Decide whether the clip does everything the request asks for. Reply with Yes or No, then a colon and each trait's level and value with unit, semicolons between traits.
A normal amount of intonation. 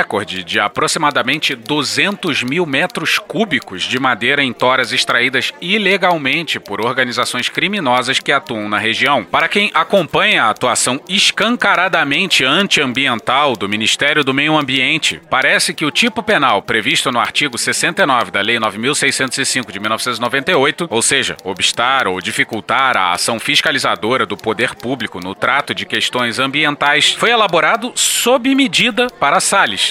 No: wide, 6.8 semitones